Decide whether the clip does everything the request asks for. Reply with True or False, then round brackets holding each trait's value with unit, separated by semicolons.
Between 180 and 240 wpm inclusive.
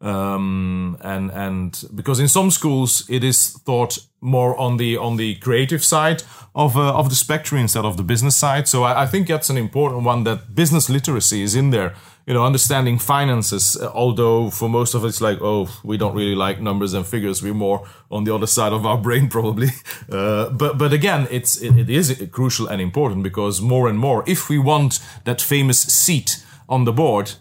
True (205 wpm)